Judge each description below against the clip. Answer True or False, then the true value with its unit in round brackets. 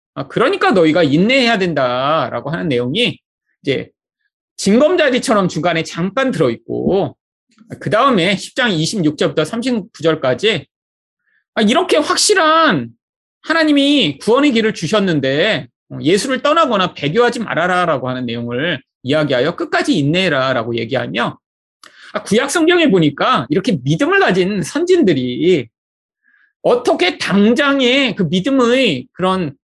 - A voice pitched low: False (210 Hz)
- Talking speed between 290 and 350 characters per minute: False (280 characters per minute)